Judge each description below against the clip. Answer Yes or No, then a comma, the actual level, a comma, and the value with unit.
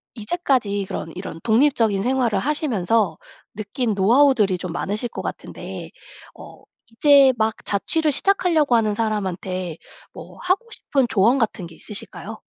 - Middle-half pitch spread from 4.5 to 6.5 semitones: Yes, average, 5.3 semitones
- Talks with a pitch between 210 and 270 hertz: Yes, high, 225 Hz